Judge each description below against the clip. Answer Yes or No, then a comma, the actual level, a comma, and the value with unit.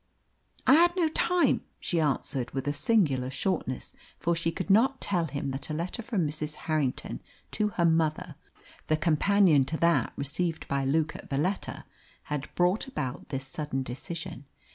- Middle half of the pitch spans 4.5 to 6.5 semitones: Yes, average, 4.9 semitones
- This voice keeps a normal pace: Yes, average, 165 wpm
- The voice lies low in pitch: No, medium, 160 Hz